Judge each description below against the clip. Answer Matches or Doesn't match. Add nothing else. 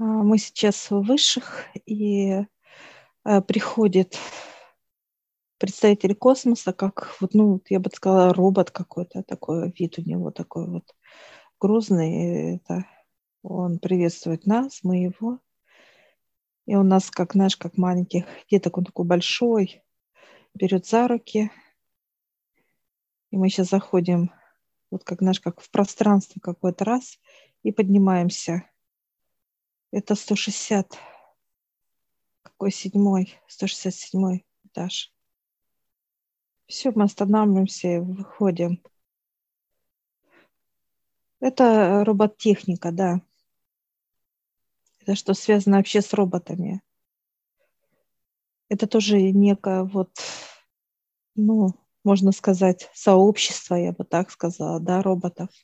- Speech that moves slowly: Matches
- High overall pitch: Matches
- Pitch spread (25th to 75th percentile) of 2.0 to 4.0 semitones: Matches